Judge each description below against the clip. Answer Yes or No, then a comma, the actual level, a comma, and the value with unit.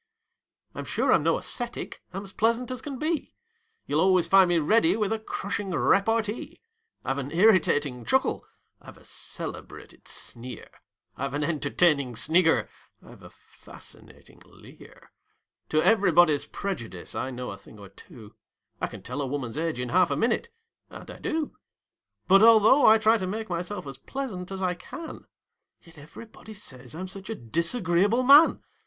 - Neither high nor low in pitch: Yes, medium, 180 Hz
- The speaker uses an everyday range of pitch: No, wide, 7.3 semitones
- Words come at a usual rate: Yes, average, 160 wpm